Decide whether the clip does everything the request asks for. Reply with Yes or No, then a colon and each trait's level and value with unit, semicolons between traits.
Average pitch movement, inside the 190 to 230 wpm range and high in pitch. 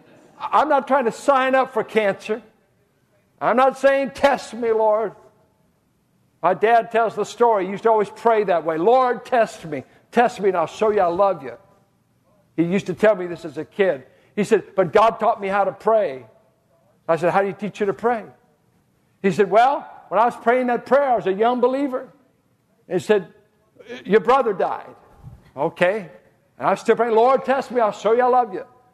Yes: average, 3.6 semitones; fast, 205 wpm; high, 215 Hz